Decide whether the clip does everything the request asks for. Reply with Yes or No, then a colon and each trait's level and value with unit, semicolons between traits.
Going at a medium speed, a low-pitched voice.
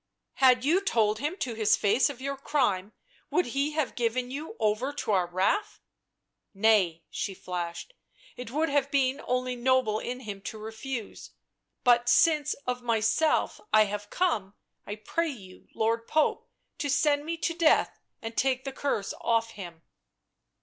No: average, 170 wpm; high, 245 Hz